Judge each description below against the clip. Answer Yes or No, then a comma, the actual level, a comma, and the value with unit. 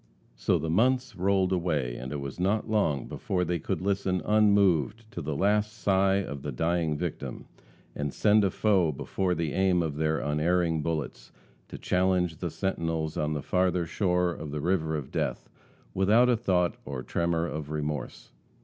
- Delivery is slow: No, average, 175 wpm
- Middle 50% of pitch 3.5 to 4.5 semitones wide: Yes, average, 4.0 semitones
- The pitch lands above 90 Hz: No, very low, 85 Hz